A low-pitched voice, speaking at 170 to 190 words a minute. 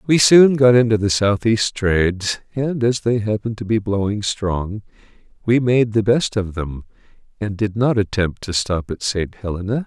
Yes: low, 105 Hz; average, 180 wpm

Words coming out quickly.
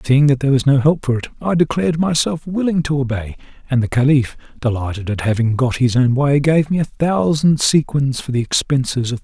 Yes: fast, 225 wpm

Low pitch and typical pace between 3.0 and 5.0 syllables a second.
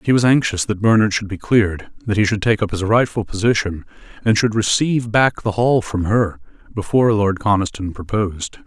No: low, 105 Hz; 5.5 syllables/s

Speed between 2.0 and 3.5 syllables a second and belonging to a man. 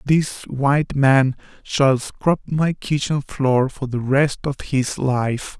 Yes: 3.2 syllables/s; male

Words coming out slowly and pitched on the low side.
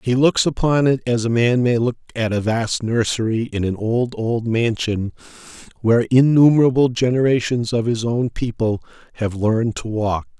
No: average, 165 wpm; low, 120 Hz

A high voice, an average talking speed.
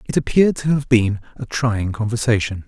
No: low, 115 Hz; average, 180 wpm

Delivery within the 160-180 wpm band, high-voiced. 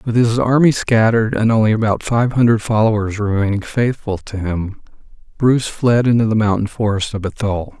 No: average, 170 wpm; low, 110 Hz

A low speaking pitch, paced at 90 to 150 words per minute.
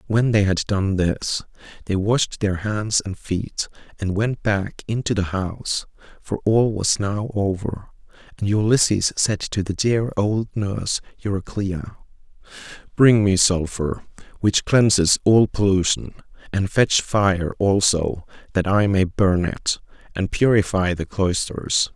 Yes: low, 100 Hz; average, 140 wpm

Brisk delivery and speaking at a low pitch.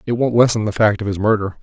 Yes: fast, 295 wpm; low, 110 Hz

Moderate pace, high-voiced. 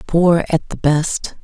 No: average, 165 wpm; medium, 160 Hz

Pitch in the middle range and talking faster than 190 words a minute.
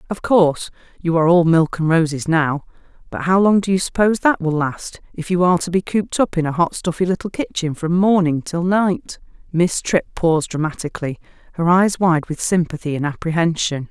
Yes: medium, 170 Hz; average, 200 wpm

